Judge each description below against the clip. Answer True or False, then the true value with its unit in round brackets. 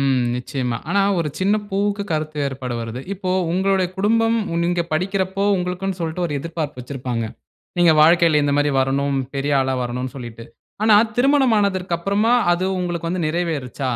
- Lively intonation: True (5.8 semitones)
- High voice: False (170 Hz)